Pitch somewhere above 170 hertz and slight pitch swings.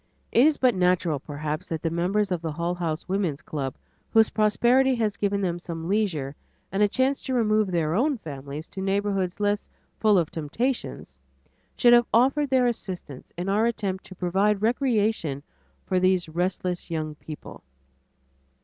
No: high, 190 Hz; average, 4.8 semitones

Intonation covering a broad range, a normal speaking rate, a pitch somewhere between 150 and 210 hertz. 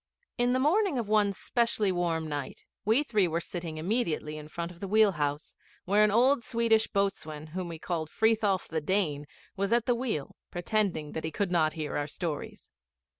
Yes: wide, 5.7 semitones; average, 190 wpm; medium, 185 Hz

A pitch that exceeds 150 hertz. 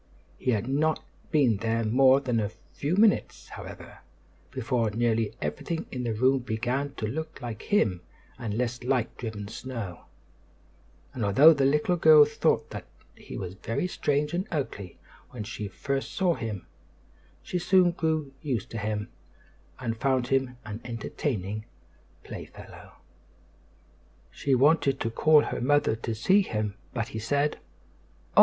No: low, 125 Hz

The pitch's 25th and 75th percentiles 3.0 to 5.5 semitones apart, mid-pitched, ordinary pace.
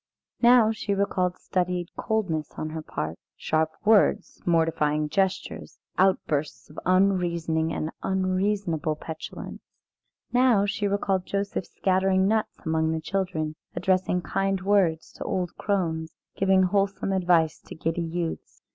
No: average, 3.4 semitones; medium, 180 Hz; slow, 125 wpm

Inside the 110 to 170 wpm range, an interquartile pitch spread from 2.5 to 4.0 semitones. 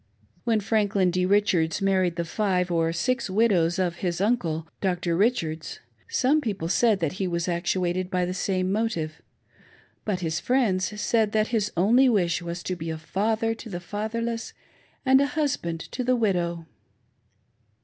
No: average, 165 wpm; average, 4.4 semitones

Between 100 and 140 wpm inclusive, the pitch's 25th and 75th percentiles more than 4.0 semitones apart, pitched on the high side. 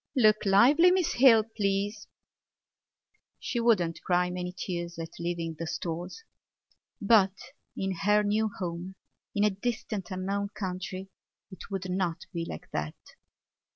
No: slow, 135 wpm; average, 3.1 semitones; high, 195 Hz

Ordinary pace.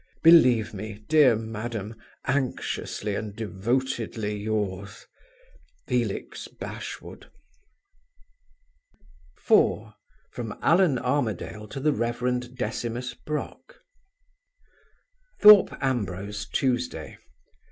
No: slow, 75 wpm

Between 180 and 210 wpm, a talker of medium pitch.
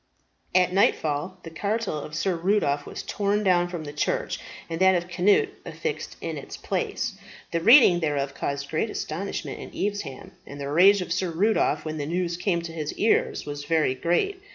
Yes: average, 185 wpm; medium, 175 Hz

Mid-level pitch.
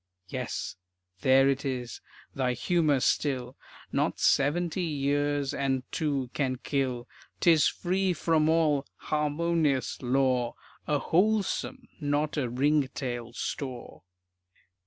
Yes: medium, 145 Hz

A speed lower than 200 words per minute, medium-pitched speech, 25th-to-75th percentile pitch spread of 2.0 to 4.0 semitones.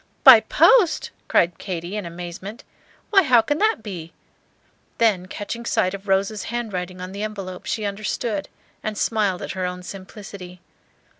No: average, 150 wpm; high, 200 Hz; average, 3.1 semitones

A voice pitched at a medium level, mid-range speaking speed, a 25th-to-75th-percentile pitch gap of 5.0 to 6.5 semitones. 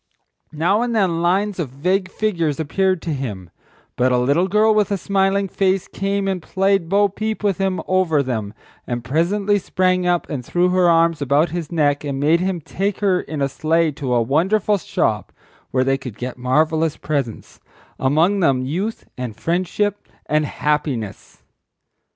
Yes: medium, 170 Hz; average, 170 wpm; wide, 5.4 semitones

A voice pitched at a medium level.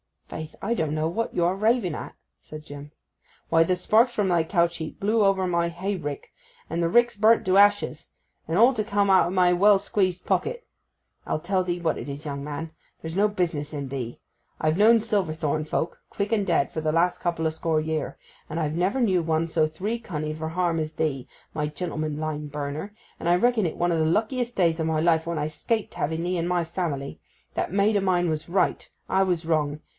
Yes: medium, 170 Hz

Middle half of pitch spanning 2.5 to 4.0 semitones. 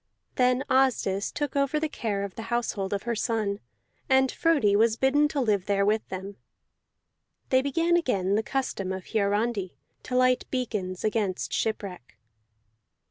No: average, 4.7 semitones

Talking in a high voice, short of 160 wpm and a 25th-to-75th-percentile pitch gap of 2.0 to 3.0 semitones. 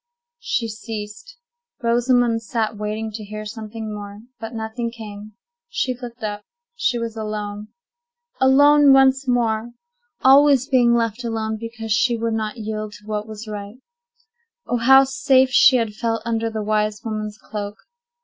Yes: high, 225 Hz; average, 150 wpm; narrow, 2.4 semitones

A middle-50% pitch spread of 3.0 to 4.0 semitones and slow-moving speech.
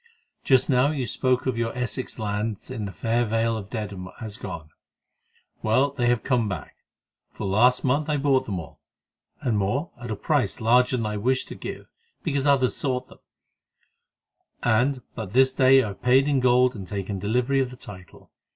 No: average, 3.7 semitones; average, 190 wpm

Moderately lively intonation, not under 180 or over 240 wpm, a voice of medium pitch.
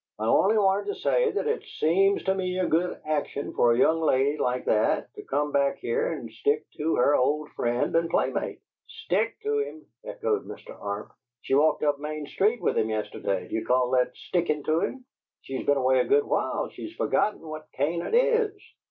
No: wide, 7.2 semitones; average, 200 wpm; medium, 155 Hz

